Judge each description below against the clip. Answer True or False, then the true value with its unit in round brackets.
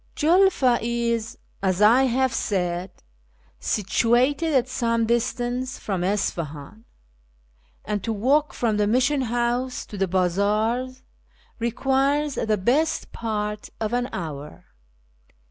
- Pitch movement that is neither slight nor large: True (3.6 semitones)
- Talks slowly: True (110 wpm)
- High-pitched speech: True (235 Hz)